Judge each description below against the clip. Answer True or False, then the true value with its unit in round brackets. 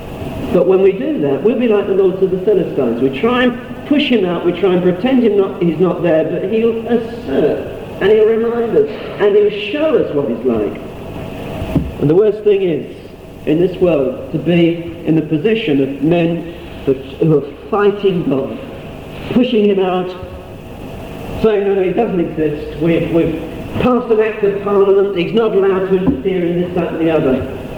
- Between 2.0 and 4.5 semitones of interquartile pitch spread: False (5.3 semitones)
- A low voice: False (190 Hz)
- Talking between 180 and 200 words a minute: True (185 wpm)